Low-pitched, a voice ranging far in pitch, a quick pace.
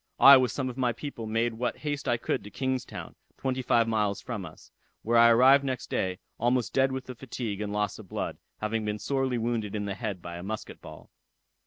No: low, 115 Hz; average, 3.5 semitones; fast, 225 wpm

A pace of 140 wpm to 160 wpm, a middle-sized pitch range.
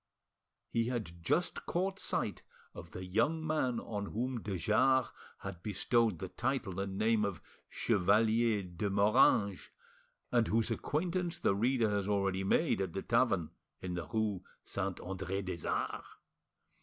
Yes: average, 145 wpm; average, 3.8 semitones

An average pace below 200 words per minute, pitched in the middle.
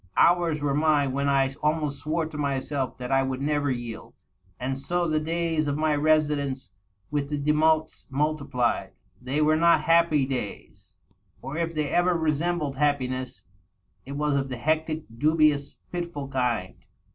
Yes: average, 155 wpm; medium, 150 Hz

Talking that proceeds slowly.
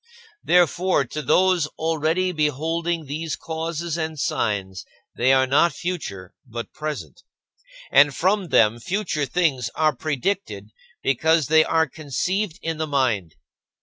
Yes: slow, 125 wpm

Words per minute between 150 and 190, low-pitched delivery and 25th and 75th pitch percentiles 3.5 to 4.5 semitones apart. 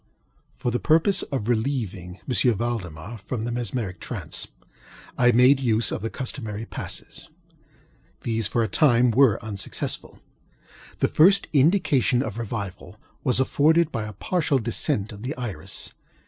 No: average, 140 wpm; low, 120 Hz; average, 3.8 semitones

